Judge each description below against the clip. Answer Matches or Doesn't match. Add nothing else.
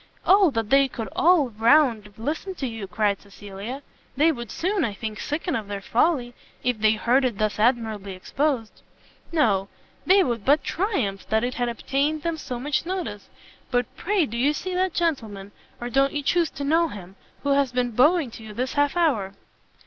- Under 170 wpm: Doesn't match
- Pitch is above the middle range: Matches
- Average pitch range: Doesn't match